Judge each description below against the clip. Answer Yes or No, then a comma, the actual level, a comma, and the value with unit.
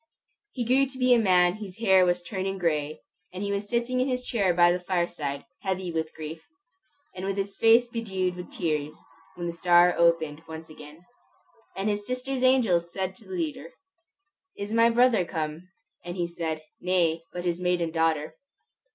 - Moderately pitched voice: Yes, medium, 180 Hz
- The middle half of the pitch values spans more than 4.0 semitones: Yes, average, 4.9 semitones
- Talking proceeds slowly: No, average, 175 wpm